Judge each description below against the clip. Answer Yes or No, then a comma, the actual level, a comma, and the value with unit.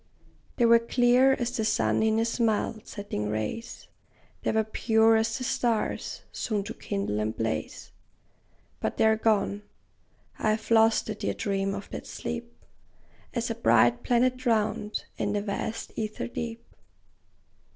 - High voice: Yes, high, 220 Hz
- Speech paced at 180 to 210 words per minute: No, average, 150 wpm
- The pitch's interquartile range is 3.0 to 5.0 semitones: No, narrow, 2.6 semitones